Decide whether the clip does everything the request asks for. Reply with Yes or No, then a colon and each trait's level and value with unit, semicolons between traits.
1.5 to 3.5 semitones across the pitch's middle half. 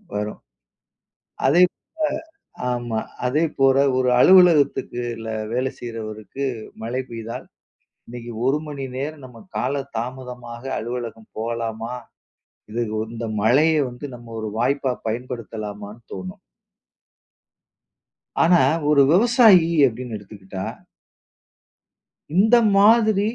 No: average, 4.0 semitones